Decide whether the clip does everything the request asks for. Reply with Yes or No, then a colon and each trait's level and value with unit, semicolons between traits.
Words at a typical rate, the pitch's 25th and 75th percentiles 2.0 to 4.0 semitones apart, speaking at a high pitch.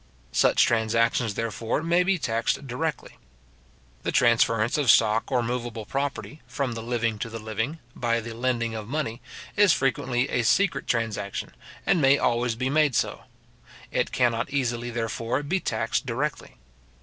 No: average, 150 wpm; average, 3.3 semitones; low, 120 Hz